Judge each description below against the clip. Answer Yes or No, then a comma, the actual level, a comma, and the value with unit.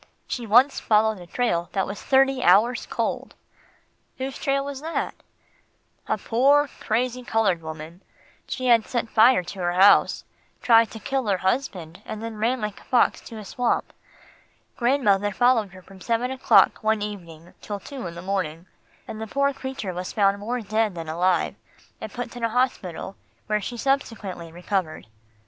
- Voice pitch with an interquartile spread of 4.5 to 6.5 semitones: Yes, average, 4.8 semitones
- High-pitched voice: Yes, high, 220 Hz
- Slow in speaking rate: No, average, 170 wpm